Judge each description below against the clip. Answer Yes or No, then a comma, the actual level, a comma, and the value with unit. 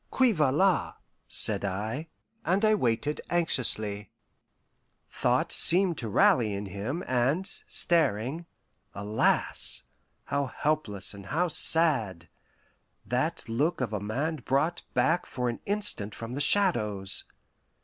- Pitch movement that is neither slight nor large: No, wide, 7.9 semitones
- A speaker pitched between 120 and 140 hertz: Yes, low, 135 Hz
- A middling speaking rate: No, slow, 120 wpm